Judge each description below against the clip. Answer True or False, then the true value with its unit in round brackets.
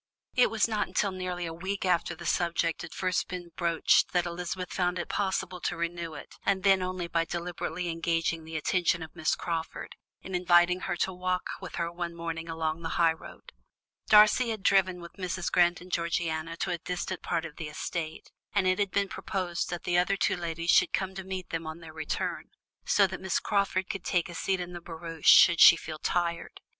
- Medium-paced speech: False (210 wpm)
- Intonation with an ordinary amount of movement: False (1.8 semitones)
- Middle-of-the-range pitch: True (175 Hz)